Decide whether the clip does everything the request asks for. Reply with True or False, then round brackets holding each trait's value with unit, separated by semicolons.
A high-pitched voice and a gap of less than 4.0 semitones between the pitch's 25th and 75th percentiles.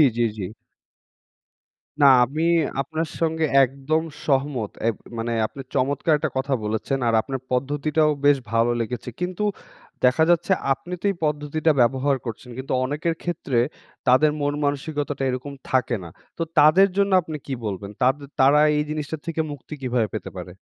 False (140 Hz; 3.6 semitones)